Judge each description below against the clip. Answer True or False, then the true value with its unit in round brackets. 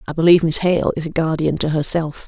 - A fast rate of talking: True (235 wpm)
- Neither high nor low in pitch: True (160 Hz)